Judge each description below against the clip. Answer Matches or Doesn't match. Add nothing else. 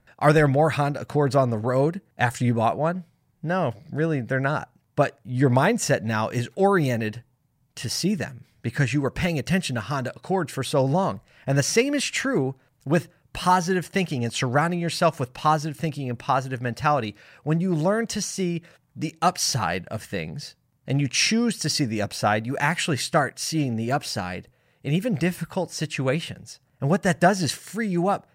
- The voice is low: Doesn't match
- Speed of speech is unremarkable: Matches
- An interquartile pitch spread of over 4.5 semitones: Matches